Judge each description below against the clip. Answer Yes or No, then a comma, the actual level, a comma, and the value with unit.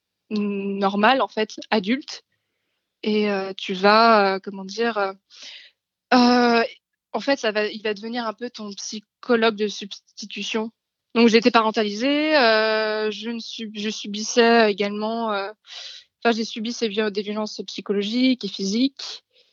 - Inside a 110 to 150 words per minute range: Yes, slow, 145 wpm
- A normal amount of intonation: No, narrow, 2.1 semitones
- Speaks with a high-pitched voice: Yes, high, 220 Hz